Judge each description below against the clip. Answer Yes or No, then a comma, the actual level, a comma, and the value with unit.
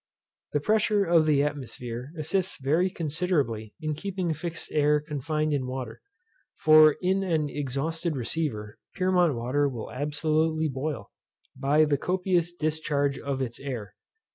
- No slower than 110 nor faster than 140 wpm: Yes, slow, 135 wpm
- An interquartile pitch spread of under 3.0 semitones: No, average, 3.3 semitones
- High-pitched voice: No, medium, 150 Hz